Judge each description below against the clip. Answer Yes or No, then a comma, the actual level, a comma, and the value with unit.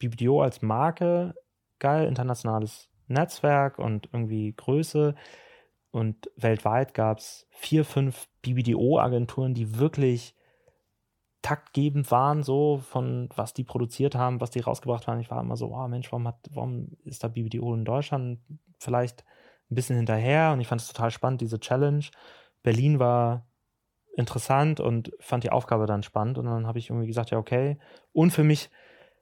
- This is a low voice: Yes, low, 125 Hz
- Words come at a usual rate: Yes, average, 155 wpm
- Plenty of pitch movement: No, average, 3.6 semitones